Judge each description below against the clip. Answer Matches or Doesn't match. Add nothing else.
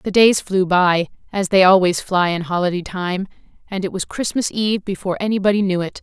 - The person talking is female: Matches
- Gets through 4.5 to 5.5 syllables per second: Doesn't match